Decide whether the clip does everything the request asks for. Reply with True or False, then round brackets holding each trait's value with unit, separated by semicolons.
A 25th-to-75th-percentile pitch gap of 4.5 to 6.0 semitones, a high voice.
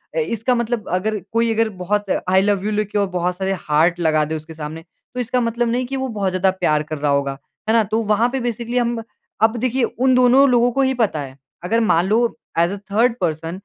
True (5.3 semitones; 215 Hz)